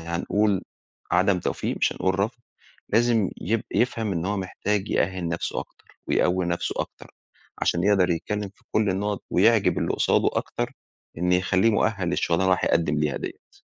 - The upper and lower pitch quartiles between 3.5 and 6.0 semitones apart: No, average, 2.7 semitones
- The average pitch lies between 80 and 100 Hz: Yes, very low, 95 Hz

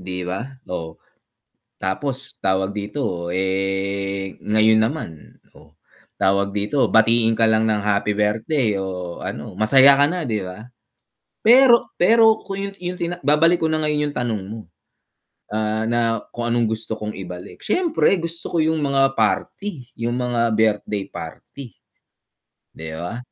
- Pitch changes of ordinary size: No, wide, 6.6 semitones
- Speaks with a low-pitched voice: Yes, low, 110 Hz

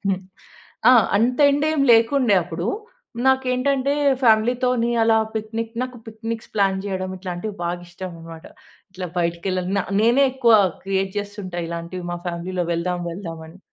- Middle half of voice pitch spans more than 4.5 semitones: Yes, average, 4.9 semitones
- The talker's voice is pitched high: Yes, high, 200 Hz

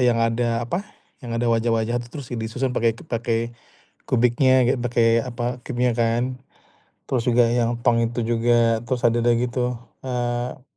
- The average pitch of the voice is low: Yes, low, 120 Hz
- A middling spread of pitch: No, narrow, 1.1 semitones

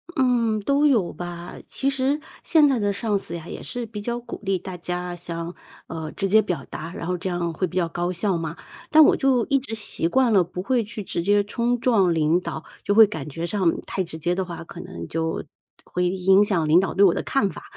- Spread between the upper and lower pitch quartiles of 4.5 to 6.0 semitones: Yes, average, 4.8 semitones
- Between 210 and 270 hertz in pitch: No, high, 190 Hz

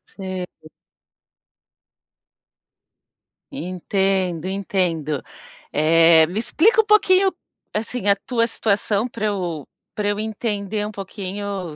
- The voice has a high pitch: Yes, high, 200 Hz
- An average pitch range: Yes, average, 3.2 semitones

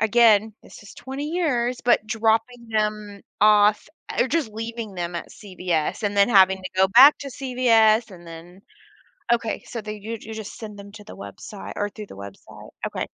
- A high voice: Yes, high, 215 Hz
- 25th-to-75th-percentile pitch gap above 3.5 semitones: No, narrow, 2.6 semitones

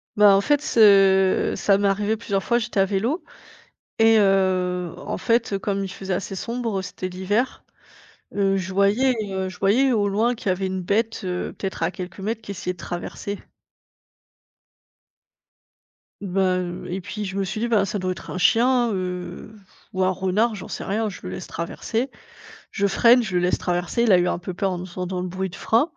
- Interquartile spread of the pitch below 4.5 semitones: Yes, average, 2.8 semitones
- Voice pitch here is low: No, high, 195 Hz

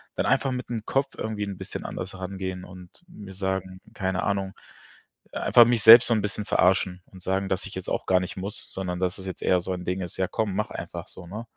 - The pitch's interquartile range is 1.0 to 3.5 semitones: Yes, narrow, 2.5 semitones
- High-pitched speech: No, very low, 95 Hz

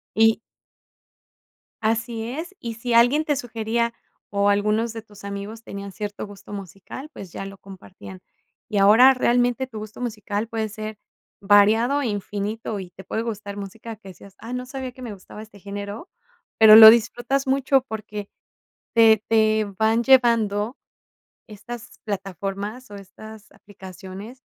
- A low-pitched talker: No, high, 220 Hz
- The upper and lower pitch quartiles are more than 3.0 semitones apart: No, average, 2.7 semitones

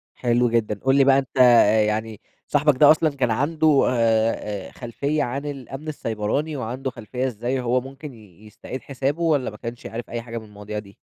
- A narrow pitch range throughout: No, average, 3.7 semitones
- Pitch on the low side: Yes, low, 125 Hz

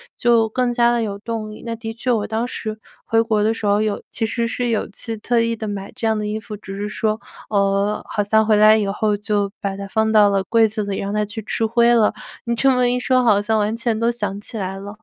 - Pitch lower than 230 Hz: Yes, high, 215 Hz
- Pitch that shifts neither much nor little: No, narrow, 1.9 semitones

